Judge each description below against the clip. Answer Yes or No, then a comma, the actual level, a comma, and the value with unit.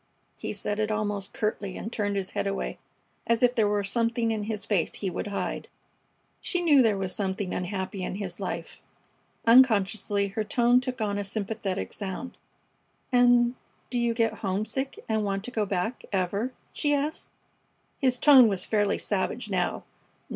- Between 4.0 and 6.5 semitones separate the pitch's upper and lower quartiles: No, average, 3.2 semitones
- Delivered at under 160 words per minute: No, average, 170 wpm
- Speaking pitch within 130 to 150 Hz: No, high, 215 Hz